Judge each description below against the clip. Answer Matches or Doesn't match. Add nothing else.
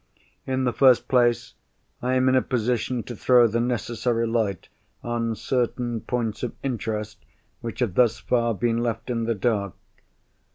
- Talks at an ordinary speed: Matches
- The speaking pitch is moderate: Doesn't match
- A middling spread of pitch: Doesn't match